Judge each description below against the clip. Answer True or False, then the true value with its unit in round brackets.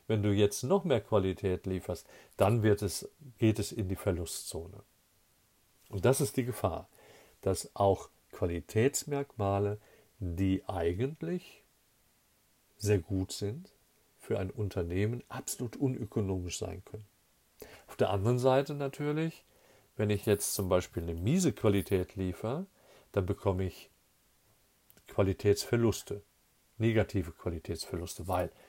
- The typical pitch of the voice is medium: False (100 Hz)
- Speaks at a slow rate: True (115 wpm)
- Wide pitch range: False (3.6 semitones)